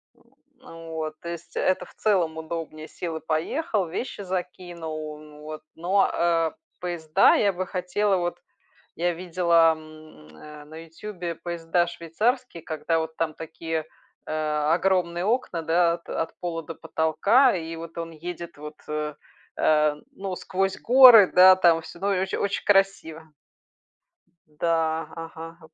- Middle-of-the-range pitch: Yes, medium, 165 Hz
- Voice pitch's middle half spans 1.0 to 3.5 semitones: Yes, narrow, 2.4 semitones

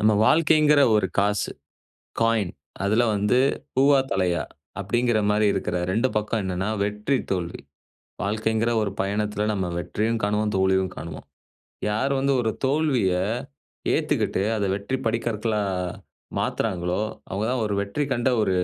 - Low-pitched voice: Yes, low, 105 Hz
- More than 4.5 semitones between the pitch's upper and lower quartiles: No, average, 2.9 semitones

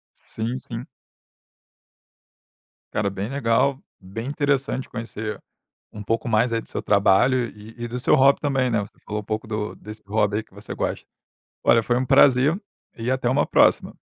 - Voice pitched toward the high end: No, low, 115 Hz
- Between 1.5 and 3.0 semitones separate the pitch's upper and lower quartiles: No, average, 3.4 semitones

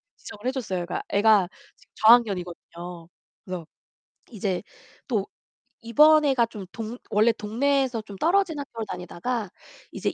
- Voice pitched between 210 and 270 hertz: Yes, high, 220 Hz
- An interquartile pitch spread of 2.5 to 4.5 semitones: No, average, 5.2 semitones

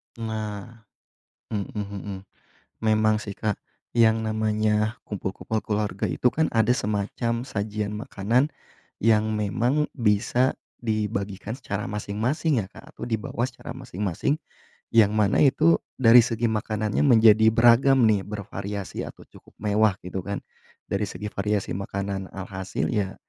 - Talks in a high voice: No, low, 110 Hz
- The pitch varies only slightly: Yes, narrow, 2.2 semitones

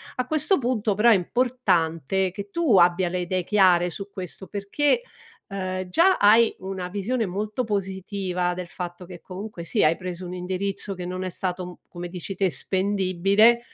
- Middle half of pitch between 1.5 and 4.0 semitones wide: Yes, narrow, 2.6 semitones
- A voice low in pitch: No, high, 190 Hz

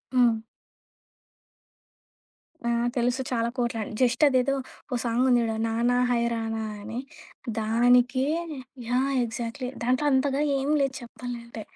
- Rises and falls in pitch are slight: Yes, narrow, 1.8 semitones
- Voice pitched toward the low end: No, high, 240 Hz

